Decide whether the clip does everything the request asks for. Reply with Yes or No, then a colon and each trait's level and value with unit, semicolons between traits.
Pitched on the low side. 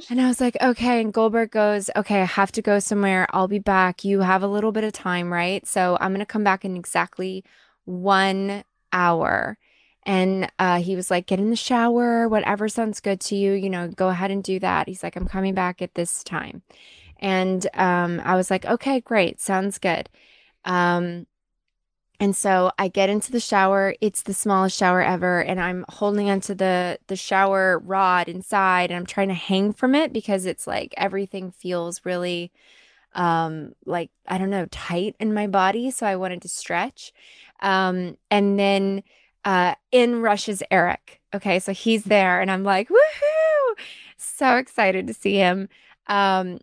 No: high, 195 Hz